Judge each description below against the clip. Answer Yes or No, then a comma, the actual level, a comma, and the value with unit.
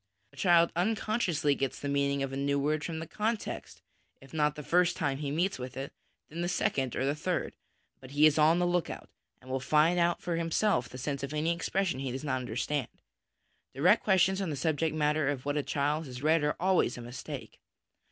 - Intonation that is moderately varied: Yes, average, 3.8 semitones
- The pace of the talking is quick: Yes, fast, 220 wpm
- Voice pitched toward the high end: No, medium, 150 Hz